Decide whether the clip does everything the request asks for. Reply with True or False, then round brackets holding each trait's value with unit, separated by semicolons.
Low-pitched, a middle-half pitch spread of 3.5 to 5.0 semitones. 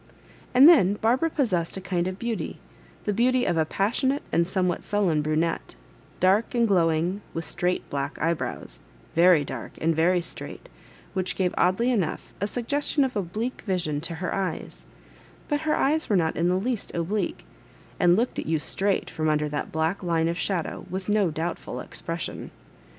False (185 Hz; 4.5 semitones)